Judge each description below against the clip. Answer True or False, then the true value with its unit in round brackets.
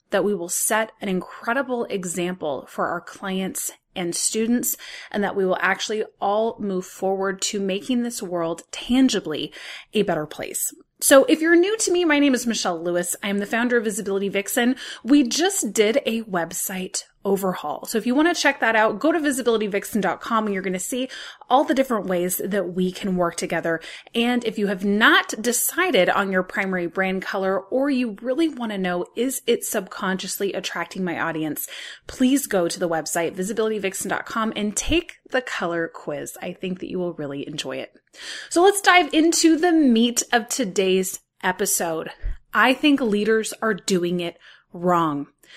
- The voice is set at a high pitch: True (210 Hz)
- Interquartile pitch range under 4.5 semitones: False (5.6 semitones)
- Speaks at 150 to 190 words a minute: True (180 wpm)